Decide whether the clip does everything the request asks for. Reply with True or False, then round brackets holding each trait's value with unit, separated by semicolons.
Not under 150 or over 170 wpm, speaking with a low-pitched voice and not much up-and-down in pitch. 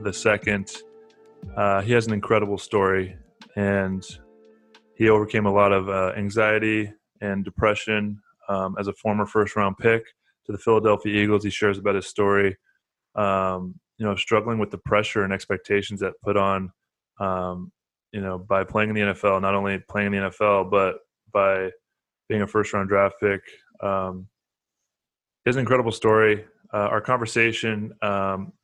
True (160 wpm; 100 Hz; 1.7 semitones)